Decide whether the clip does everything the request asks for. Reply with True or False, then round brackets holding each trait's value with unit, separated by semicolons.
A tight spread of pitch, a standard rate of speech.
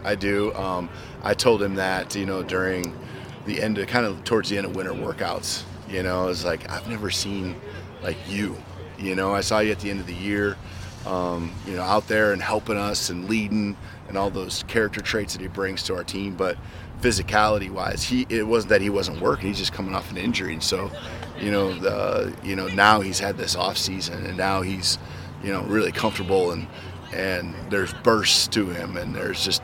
False (2.1 semitones; 220 wpm)